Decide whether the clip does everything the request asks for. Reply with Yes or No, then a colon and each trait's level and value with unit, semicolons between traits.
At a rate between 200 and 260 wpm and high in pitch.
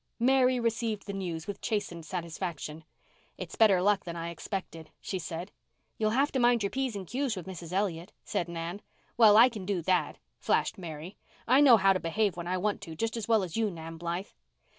Yes: fast, 205 wpm; high, 195 Hz